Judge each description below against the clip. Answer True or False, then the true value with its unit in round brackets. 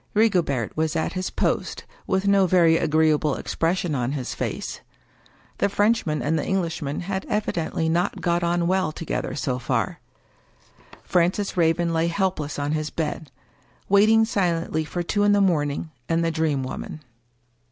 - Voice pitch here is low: False (165 Hz)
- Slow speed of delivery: False (150 wpm)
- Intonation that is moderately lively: True (3.6 semitones)